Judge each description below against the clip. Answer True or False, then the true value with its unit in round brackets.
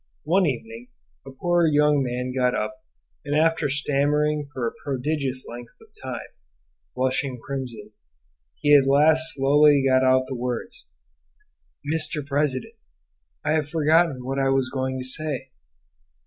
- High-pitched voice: False (140 Hz)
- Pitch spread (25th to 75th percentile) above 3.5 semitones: False (2.6 semitones)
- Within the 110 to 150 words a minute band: True (140 wpm)